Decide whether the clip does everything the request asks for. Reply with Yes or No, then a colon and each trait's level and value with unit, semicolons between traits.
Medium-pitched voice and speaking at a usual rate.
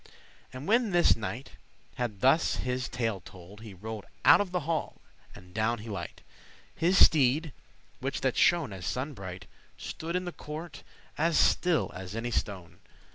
No: low, 125 Hz; average, 165 wpm